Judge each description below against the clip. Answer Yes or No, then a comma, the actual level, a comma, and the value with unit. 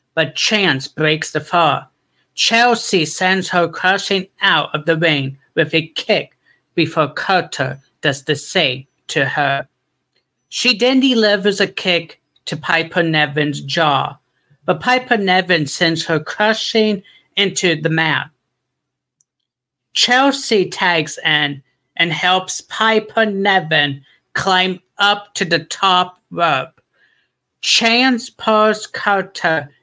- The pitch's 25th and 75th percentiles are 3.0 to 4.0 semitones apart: No, average, 5.3 semitones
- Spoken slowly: Yes, slow, 115 wpm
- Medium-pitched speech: Yes, medium, 170 Hz